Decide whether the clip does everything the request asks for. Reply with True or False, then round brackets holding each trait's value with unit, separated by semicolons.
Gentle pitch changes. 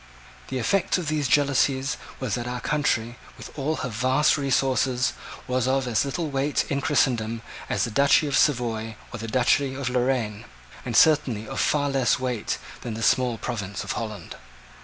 False (3.3 semitones)